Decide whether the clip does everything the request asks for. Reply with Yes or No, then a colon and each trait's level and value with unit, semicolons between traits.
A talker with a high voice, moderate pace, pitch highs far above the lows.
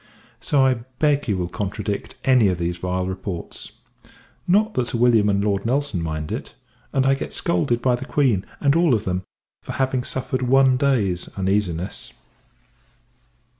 No: low, 115 Hz; average, 165 wpm; wide, 6.1 semitones